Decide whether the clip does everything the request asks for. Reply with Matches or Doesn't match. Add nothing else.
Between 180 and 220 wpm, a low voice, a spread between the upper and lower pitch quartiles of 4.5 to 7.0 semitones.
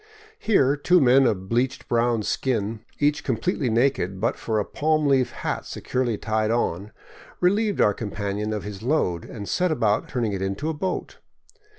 Doesn't match